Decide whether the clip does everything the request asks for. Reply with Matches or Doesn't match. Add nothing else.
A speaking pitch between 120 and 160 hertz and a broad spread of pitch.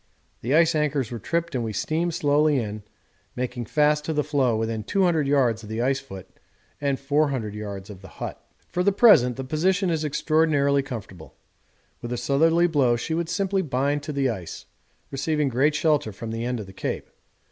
Doesn't match